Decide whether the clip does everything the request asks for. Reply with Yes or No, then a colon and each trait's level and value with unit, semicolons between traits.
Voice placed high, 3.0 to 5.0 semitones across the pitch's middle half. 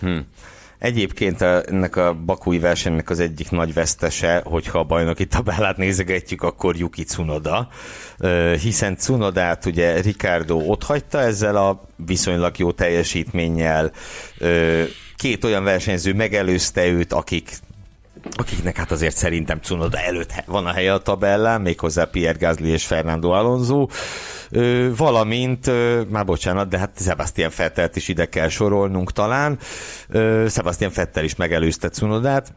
No: very low, 90 Hz; average, 3.6 semitones